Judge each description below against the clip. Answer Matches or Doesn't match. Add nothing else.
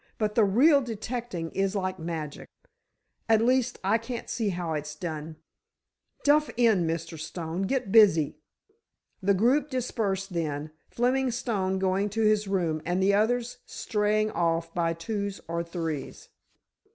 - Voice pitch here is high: Matches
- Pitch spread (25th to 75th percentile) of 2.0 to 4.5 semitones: Doesn't match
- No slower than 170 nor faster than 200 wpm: Doesn't match